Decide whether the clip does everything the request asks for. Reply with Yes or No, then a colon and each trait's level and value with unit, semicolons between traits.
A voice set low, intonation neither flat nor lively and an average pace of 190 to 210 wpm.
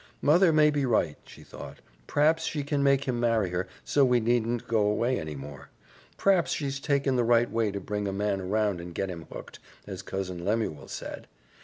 No: low, 115 Hz; wide, 6.1 semitones; average, 200 wpm